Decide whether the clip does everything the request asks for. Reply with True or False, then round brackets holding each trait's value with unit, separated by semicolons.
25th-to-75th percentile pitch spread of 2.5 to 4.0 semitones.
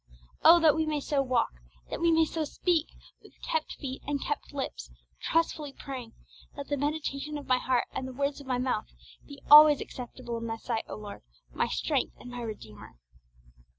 True (3.6 semitones)